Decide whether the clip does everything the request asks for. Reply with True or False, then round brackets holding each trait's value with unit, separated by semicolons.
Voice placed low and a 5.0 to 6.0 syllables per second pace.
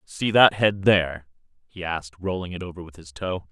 True (90 Hz; 5.3 syllables/s)